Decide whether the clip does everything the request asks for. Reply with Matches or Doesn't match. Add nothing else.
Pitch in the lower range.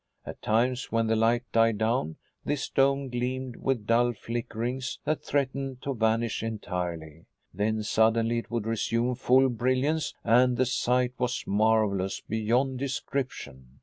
Matches